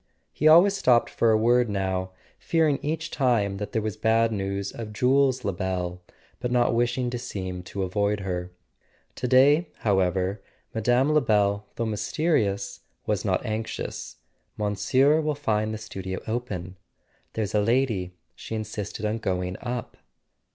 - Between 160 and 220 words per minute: No, average, 145 wpm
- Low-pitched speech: Yes, low, 110 Hz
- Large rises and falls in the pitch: No, average, 4.2 semitones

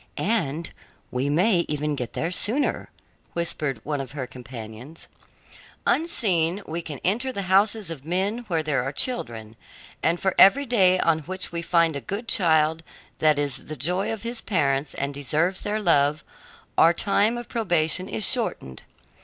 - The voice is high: No, medium, 165 Hz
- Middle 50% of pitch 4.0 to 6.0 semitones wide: Yes, wide, 5.5 semitones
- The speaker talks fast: No, average, 160 wpm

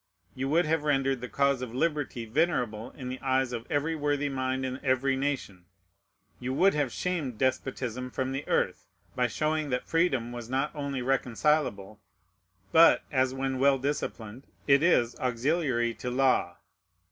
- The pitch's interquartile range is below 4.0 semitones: Yes, average, 2.7 semitones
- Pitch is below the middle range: Yes, low, 130 Hz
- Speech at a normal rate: Yes, average, 160 wpm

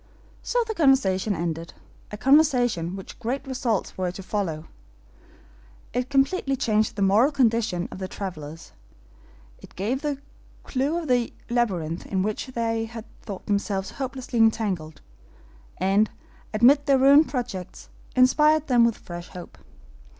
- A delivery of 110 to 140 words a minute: Yes, slow, 135 wpm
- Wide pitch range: Yes, wide, 5.9 semitones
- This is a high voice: Yes, high, 225 Hz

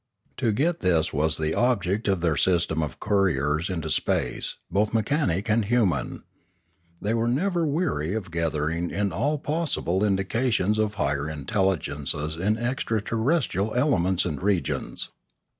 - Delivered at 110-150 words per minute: Yes, average, 140 wpm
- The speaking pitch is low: Yes, low, 100 Hz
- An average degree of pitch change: No, wide, 5.9 semitones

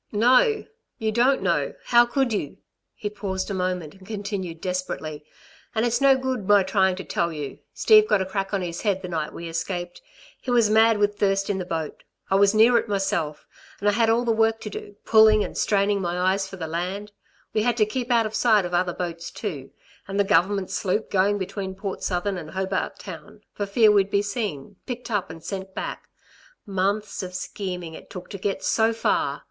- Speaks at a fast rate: Yes, fast, 210 wpm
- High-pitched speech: Yes, high, 200 Hz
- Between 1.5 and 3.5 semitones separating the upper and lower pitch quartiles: Yes, average, 3.0 semitones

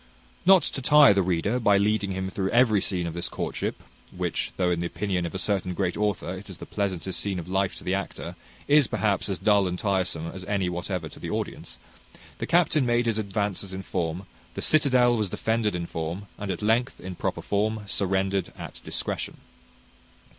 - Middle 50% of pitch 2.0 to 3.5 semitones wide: Yes, average, 2.9 semitones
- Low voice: Yes, low, 100 Hz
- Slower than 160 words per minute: No, average, 200 wpm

